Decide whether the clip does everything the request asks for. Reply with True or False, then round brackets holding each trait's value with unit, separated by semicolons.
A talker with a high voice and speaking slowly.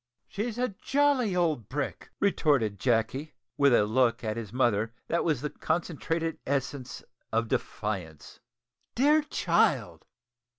False (140 Hz; 125 wpm)